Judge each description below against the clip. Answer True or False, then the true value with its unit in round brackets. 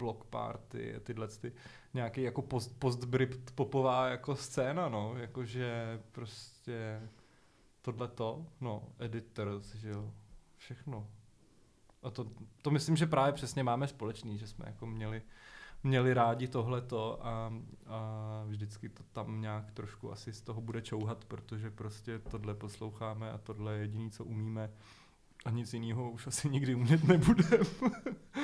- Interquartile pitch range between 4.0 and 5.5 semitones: False (2.8 semitones)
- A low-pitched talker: True (115 Hz)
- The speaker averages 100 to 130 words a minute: False (140 wpm)